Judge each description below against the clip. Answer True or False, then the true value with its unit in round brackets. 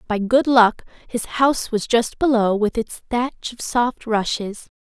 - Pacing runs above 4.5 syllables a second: False (4.1 syllables/s)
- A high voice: True (230 Hz)